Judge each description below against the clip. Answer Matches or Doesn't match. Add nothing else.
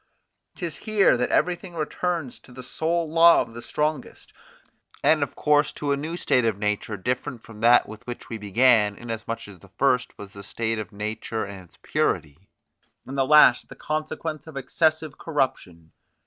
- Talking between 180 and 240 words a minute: Matches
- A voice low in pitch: Matches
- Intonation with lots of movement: Matches